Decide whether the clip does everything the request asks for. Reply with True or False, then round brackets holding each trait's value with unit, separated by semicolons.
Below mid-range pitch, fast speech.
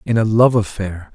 True (105 Hz; 210 wpm)